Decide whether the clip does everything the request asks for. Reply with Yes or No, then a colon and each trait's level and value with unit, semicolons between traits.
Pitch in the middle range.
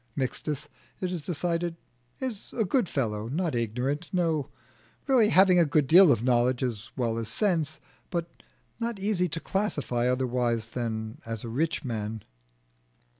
Yes: medium, 145 Hz